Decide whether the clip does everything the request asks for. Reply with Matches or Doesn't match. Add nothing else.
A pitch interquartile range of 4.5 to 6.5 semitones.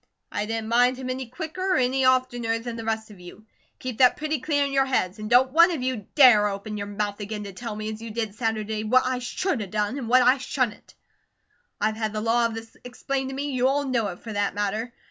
Doesn't match